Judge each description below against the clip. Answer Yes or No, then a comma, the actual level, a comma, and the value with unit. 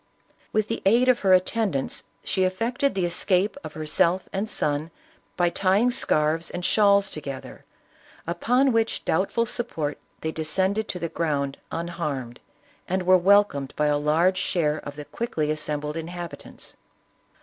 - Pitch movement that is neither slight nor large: Yes, average, 4.8 semitones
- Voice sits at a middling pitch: Yes, medium, 175 Hz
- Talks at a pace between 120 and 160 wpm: Yes, average, 150 wpm